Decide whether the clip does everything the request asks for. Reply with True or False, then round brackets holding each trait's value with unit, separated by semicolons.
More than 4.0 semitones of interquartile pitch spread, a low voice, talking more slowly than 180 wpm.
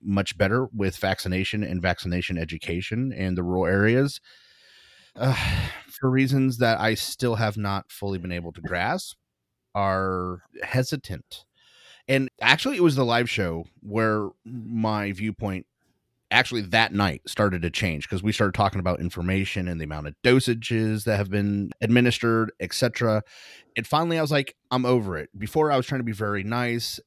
True (4.5 semitones; 110 Hz; 165 wpm)